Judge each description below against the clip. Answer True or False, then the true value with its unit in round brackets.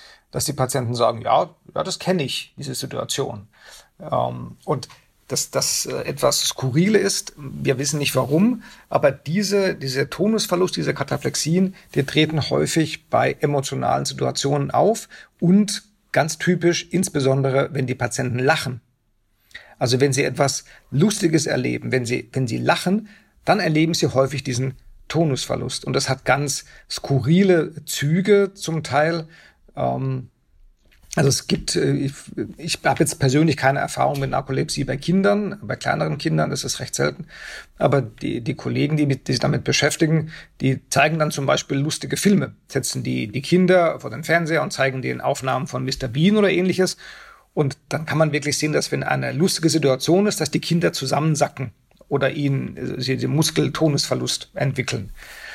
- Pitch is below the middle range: False (145 Hz)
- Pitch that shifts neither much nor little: True (4.4 semitones)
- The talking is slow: False (155 wpm)